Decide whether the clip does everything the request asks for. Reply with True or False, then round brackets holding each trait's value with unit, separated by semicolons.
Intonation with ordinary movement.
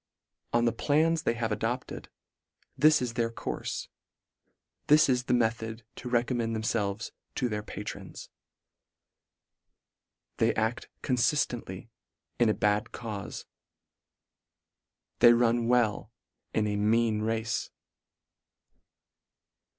False (1.9 semitones)